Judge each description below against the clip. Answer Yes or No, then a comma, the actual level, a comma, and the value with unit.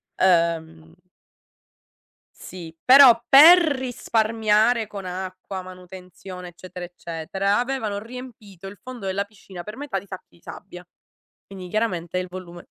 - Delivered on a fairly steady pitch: No, average, 3.9 semitones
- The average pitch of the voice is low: No, high, 195 Hz